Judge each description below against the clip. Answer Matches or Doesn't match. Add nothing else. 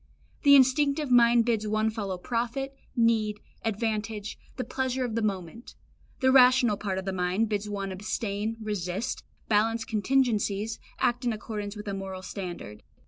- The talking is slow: Doesn't match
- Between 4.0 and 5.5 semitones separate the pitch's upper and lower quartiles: Doesn't match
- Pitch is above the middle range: Matches